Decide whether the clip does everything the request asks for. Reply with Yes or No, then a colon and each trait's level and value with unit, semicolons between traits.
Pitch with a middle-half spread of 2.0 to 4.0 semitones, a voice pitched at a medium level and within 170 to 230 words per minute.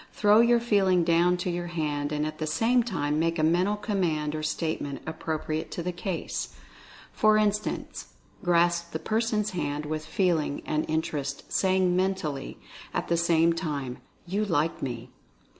No: average, 3.7 semitones; medium, 170 Hz; average, 160 wpm